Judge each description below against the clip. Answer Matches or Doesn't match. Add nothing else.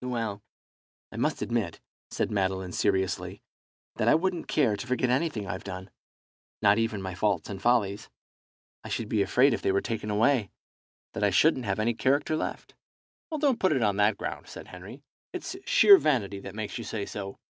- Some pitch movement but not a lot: Matches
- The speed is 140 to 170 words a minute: Doesn't match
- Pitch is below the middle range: Matches